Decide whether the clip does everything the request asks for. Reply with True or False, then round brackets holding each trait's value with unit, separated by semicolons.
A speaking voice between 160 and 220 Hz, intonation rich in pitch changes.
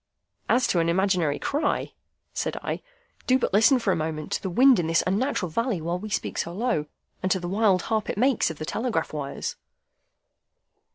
True (190 Hz; 5.7 semitones)